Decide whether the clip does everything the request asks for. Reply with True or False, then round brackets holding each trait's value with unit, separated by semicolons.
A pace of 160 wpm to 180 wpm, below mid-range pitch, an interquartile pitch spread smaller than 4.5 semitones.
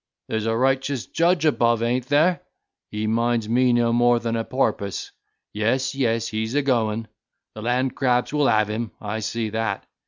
True (175 wpm; 115 Hz; 2.8 semitones)